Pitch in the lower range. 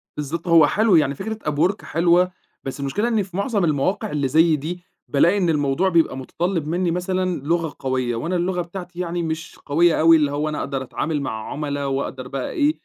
No: medium, 165 Hz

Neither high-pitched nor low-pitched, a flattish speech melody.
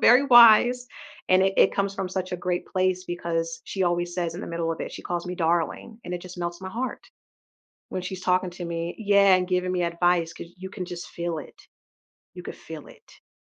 Yes: medium, 180 Hz; narrow, 1.6 semitones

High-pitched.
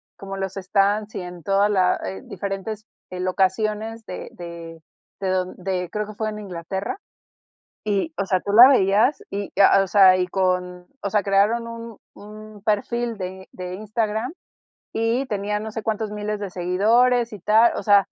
Yes: high, 200 Hz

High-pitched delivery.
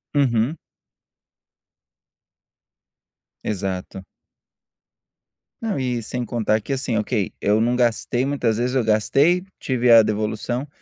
No: low, 120 Hz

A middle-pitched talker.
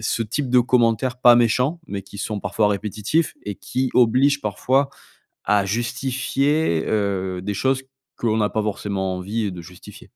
No: low, 110 Hz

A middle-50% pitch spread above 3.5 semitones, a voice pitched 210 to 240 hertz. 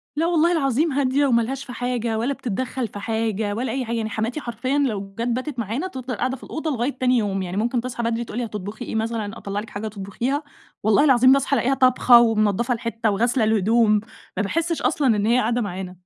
No: average, 3.2 semitones; high, 235 Hz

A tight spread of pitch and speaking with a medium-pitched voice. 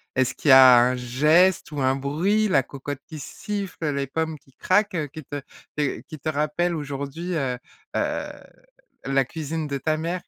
No: average, 3.3 semitones; medium, 150 Hz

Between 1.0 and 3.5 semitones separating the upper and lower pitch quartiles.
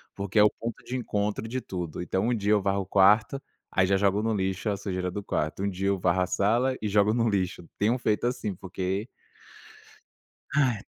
Yes: narrow, 2.6 semitones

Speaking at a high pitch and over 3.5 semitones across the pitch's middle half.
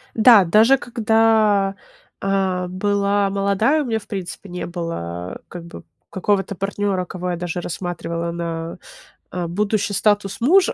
No: high, 195 Hz; average, 3.0 semitones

